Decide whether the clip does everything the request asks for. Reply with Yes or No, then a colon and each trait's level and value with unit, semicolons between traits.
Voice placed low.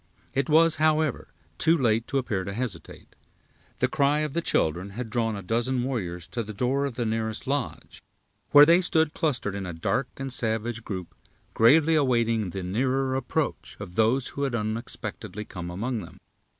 Yes: low, 120 Hz